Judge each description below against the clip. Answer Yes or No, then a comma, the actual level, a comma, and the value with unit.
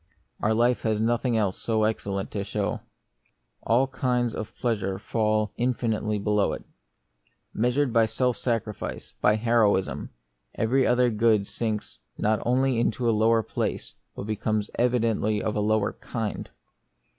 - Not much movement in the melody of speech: Yes, narrow, 2.1 semitones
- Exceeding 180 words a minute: No, average, 140 wpm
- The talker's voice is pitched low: Yes, low, 110 Hz